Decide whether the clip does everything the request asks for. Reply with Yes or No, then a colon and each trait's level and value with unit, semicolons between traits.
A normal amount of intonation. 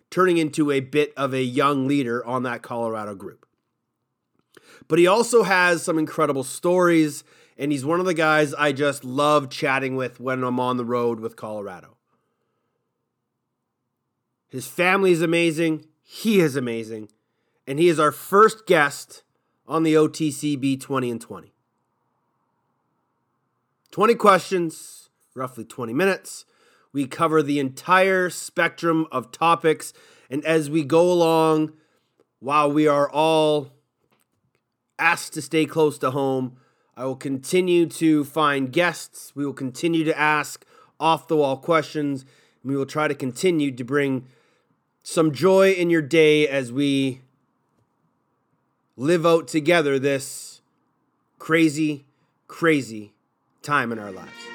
Yes: average, 3.8 semitones